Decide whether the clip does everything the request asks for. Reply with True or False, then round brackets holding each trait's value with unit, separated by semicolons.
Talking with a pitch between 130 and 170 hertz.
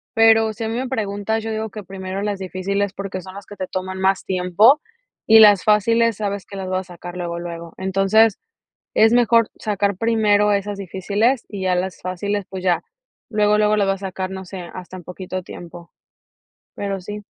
False (200 Hz)